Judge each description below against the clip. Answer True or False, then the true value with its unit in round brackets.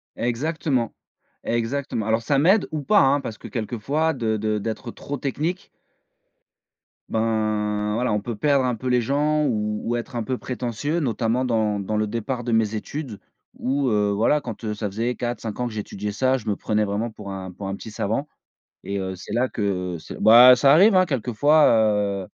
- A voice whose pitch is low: True (115 Hz)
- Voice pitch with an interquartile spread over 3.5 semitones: True (4.0 semitones)